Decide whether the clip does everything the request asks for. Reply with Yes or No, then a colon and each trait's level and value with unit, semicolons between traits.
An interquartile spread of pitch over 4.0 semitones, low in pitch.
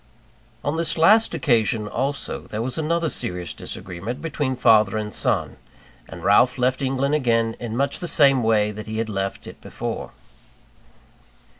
Yes: average, 4.7 semitones; low, 120 Hz